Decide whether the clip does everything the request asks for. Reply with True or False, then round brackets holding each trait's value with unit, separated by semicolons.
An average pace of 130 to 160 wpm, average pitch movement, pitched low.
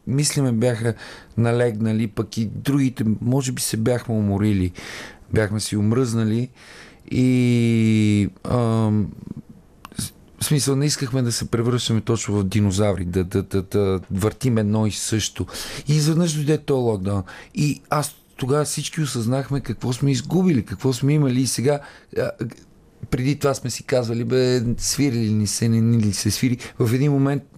True (155 wpm; 4.2 semitones; 120 Hz)